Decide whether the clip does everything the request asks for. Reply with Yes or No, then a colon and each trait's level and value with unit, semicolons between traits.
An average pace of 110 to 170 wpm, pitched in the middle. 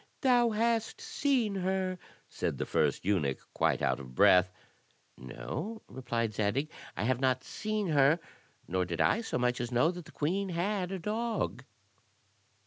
Yes: average, 155 wpm; medium, 170 Hz